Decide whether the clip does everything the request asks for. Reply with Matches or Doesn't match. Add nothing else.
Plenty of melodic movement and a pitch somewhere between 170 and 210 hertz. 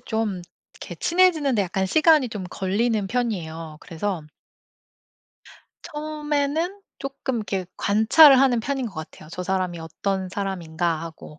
Matches